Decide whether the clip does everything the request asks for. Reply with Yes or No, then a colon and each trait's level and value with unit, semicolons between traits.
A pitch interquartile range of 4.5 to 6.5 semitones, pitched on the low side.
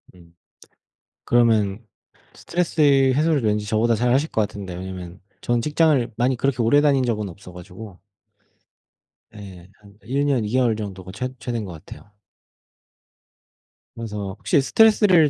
Yes: average, 5.3 semitones; low, 115 Hz